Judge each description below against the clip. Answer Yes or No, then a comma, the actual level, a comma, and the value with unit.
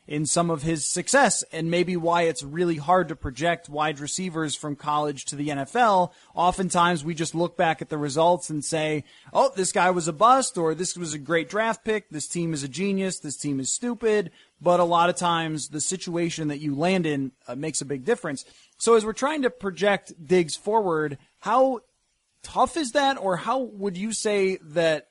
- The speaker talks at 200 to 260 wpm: Yes, fast, 205 wpm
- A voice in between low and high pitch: Yes, medium, 170 Hz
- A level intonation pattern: No, average, 4.1 semitones